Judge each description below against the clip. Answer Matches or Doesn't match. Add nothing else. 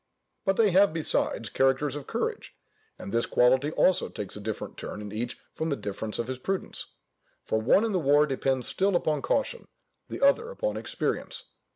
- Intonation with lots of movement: Matches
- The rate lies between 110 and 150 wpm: Doesn't match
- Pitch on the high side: Doesn't match